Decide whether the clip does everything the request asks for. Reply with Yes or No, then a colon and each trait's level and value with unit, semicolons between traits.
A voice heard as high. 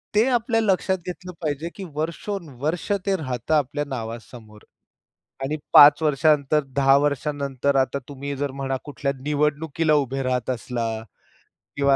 No: medium, 145 Hz